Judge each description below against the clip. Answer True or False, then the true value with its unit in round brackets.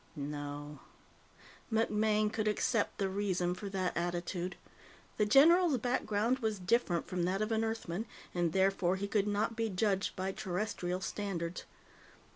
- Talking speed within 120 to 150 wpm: True (140 wpm)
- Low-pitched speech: False (200 Hz)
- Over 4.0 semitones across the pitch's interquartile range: False (3.5 semitones)